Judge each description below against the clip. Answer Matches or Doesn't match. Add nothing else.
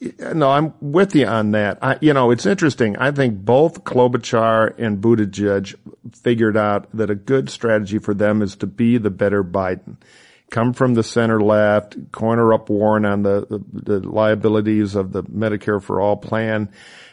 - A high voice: Doesn't match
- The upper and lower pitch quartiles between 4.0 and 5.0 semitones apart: Doesn't match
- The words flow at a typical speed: Matches